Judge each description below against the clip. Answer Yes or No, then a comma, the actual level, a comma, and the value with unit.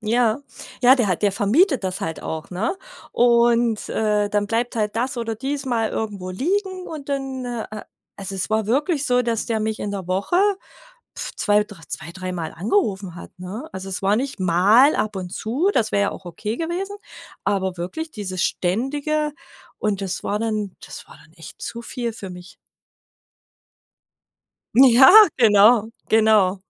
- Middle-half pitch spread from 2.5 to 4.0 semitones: No, average, 4.5 semitones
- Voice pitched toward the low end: No, high, 220 Hz